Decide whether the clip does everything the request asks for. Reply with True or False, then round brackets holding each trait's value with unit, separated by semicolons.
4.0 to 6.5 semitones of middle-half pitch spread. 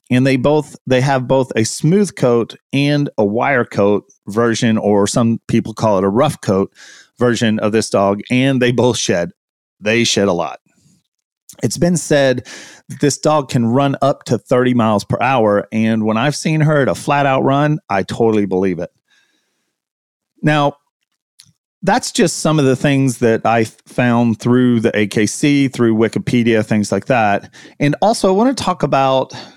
True (4.5 semitones)